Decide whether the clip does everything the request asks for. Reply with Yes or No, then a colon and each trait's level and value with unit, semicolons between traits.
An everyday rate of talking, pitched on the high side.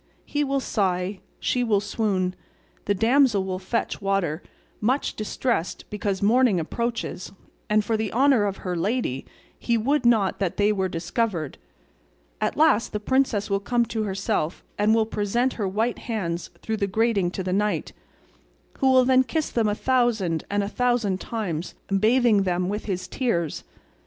Yes: average, 160 wpm; high, 210 Hz